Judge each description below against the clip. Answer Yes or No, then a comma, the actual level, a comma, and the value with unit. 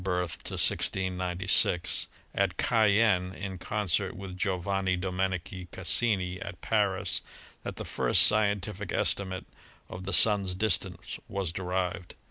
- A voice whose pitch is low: Yes, very low, 95 Hz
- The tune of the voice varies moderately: No, narrow, 1.6 semitones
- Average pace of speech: No, slow, 105 wpm